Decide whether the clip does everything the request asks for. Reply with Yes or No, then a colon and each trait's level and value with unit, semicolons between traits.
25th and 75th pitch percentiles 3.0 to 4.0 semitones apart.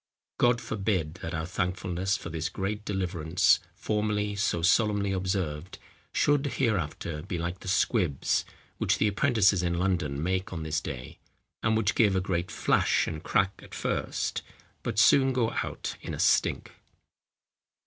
Yes: average, 3.6 semitones